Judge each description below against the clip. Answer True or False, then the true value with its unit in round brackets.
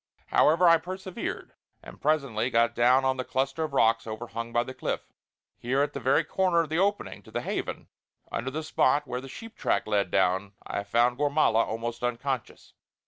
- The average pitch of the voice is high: False (130 Hz)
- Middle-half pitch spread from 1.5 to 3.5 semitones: False (4.7 semitones)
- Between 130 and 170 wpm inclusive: False (190 wpm)